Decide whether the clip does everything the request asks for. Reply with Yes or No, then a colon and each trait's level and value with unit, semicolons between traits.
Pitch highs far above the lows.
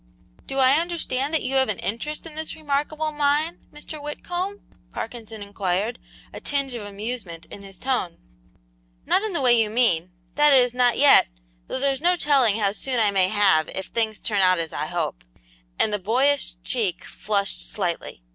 Yes: wide, 6.2 semitones